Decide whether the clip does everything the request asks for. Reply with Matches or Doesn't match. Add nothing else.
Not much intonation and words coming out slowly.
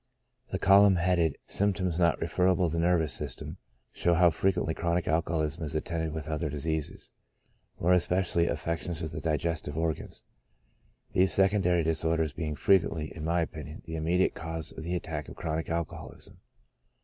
Doesn't match